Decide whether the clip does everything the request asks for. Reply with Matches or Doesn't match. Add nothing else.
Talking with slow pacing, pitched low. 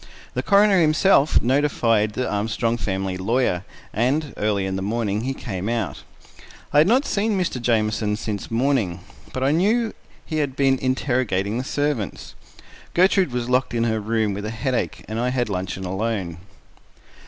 Doesn't match